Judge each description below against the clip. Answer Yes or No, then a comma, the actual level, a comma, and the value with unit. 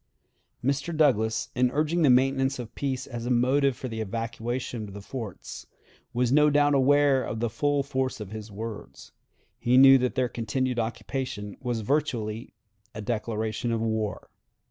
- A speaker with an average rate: Yes, average, 165 wpm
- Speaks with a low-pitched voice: Yes, low, 125 Hz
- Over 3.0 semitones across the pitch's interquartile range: Yes, average, 3.4 semitones